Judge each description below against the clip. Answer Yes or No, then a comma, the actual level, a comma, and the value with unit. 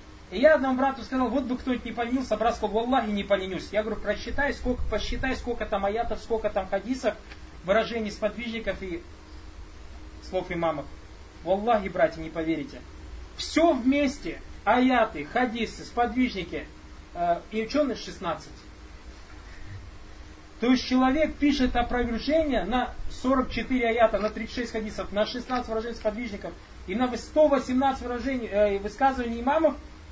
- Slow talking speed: No, average, 135 wpm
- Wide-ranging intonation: Yes, wide, 6.6 semitones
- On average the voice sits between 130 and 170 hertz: No, high, 220 Hz